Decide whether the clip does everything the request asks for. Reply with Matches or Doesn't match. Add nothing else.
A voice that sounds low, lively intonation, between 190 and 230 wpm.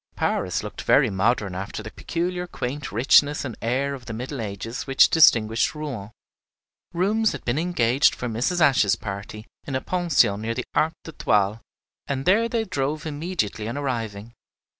Doesn't match